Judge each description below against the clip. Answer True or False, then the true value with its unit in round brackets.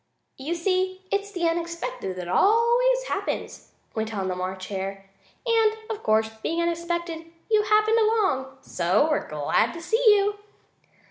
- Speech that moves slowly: False (145 wpm)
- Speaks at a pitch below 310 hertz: False (340 Hz)